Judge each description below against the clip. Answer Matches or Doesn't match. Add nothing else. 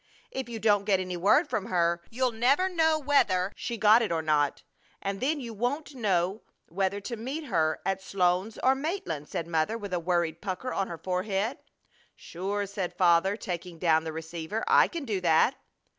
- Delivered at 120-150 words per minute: Doesn't match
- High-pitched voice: Matches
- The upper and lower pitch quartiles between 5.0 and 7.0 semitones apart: Matches